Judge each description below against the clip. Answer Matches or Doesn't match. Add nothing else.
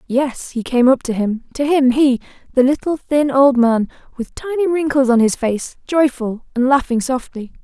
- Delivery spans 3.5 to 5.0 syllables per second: Matches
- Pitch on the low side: Doesn't match